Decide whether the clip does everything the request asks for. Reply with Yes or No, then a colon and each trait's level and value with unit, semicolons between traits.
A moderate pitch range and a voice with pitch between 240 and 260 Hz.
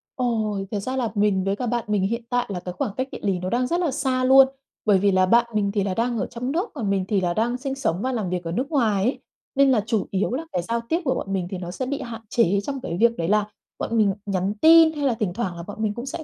No: average, 4.8 semitones; high, 225 Hz